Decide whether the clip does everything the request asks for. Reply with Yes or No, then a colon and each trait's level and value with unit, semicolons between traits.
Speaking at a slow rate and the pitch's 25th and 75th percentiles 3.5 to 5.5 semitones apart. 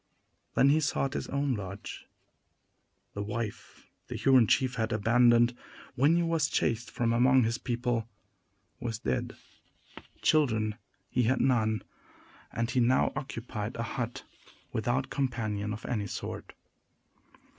No: slow, 130 wpm; average, 3.0 semitones